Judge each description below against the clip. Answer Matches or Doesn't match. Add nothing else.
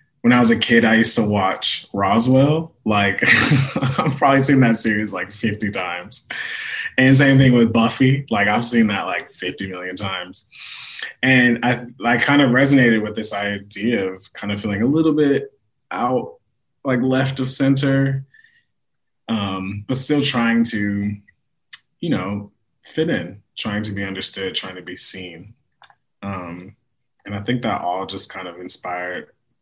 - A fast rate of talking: Doesn't match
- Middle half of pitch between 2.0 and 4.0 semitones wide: Doesn't match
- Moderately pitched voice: Doesn't match